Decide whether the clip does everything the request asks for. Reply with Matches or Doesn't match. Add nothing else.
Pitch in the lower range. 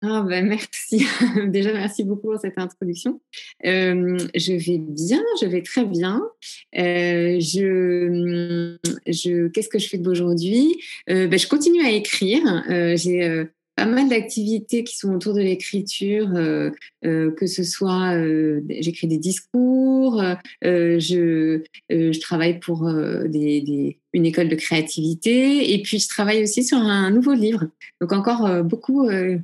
Doesn't match